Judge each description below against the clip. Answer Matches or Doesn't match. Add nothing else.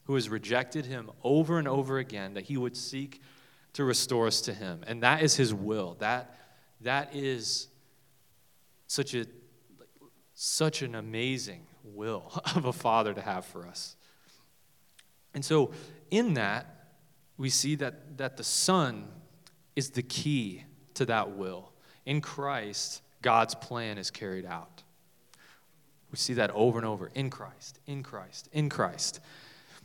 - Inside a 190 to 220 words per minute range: Doesn't match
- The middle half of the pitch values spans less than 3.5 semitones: Doesn't match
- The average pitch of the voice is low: Matches